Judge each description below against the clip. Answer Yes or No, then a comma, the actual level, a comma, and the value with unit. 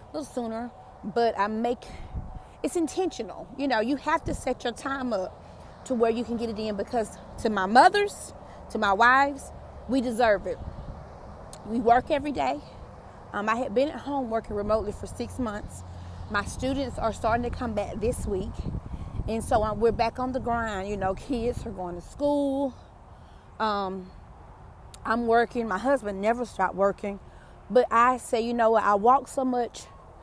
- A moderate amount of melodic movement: Yes, average, 3.7 semitones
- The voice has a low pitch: No, high, 235 Hz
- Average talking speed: Yes, average, 175 wpm